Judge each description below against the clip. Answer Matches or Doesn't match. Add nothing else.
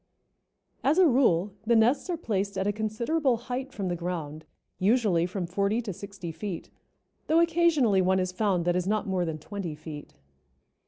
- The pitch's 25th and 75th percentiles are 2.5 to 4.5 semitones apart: Doesn't match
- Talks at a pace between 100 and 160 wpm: Doesn't match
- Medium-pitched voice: Doesn't match